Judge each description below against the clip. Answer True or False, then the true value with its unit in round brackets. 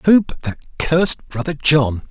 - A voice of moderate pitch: True (150 Hz)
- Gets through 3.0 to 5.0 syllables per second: True (4.6 syllables/s)